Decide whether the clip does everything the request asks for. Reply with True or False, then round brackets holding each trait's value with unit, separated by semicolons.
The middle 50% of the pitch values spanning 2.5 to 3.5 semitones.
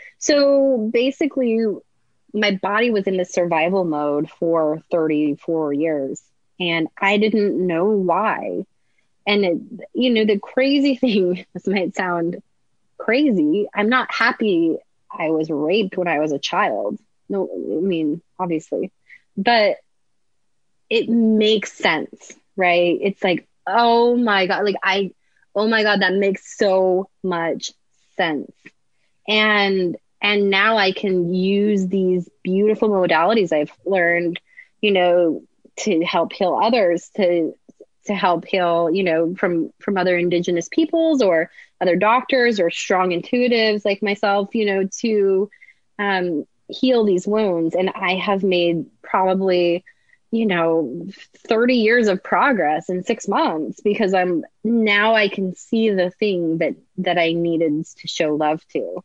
False (4.1 semitones)